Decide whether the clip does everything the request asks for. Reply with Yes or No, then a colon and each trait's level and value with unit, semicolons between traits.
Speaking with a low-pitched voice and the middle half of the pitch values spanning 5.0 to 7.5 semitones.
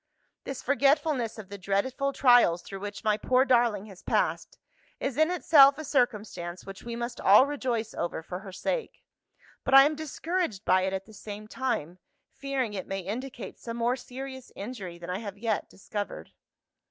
No: high, 230 Hz; wide, 5.4 semitones